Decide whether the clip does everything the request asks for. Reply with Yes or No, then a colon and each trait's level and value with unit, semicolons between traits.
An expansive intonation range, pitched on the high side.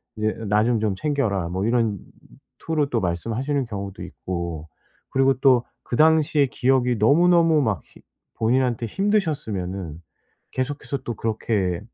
No: wide, 6.0 semitones; low, 120 Hz